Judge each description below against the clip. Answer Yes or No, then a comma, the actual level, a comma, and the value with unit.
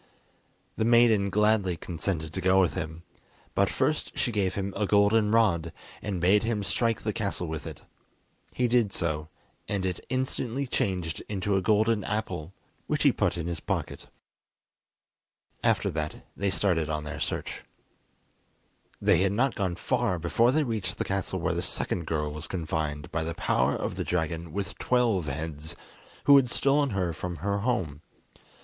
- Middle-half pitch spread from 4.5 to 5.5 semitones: Yes, average, 4.8 semitones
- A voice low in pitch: Yes, very low, 95 Hz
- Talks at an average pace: Yes, average, 170 wpm